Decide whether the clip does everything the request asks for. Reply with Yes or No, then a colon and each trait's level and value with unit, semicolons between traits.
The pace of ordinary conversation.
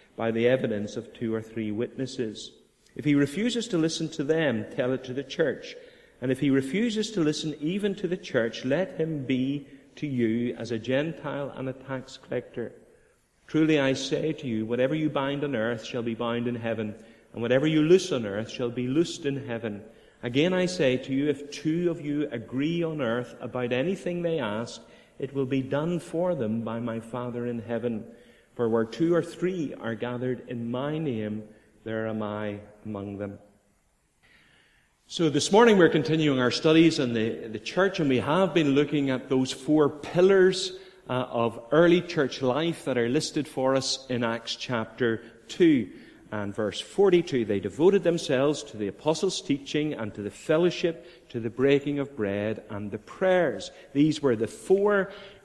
Yes: average, 185 wpm